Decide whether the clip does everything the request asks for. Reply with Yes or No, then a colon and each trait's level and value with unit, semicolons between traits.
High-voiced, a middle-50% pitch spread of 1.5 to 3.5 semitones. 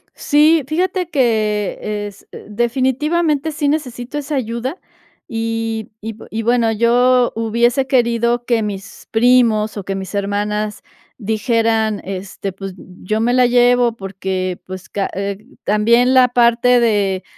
Yes: high, 230 Hz; average, 3.1 semitones